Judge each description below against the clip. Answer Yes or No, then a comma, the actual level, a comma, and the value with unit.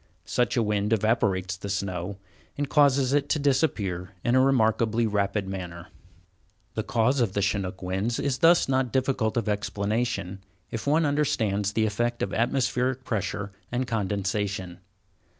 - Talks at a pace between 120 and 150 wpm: Yes, average, 145 wpm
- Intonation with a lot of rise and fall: No, average, 4.4 semitones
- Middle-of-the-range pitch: No, low, 110 Hz